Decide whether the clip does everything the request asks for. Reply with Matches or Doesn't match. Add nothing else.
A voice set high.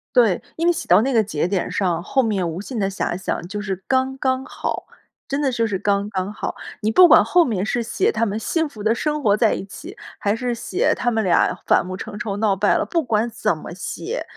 Matches